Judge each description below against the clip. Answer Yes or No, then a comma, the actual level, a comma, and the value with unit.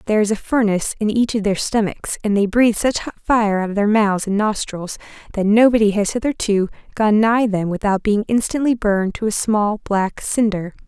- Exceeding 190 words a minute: Yes, fast, 205 wpm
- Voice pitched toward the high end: Yes, high, 210 Hz